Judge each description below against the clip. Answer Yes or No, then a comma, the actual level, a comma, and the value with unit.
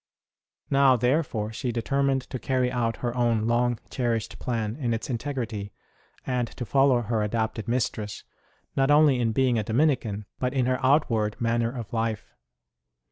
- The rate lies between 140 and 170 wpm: Yes, average, 155 wpm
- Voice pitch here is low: Yes, low, 120 Hz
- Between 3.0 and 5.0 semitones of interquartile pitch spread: No, narrow, 2.6 semitones